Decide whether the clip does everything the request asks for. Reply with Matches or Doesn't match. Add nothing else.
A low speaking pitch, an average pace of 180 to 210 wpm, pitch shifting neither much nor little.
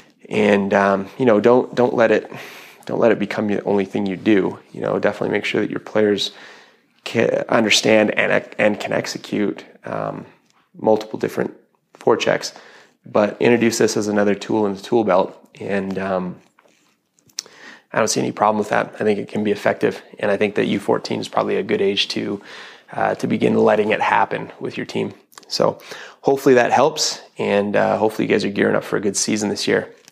Doesn't match